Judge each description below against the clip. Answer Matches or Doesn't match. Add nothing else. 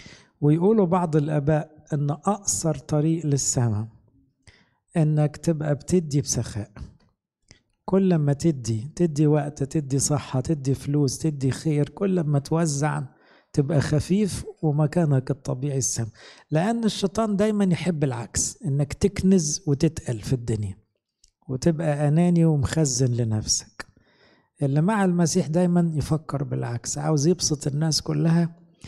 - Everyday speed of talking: Doesn't match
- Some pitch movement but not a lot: Matches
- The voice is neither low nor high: Matches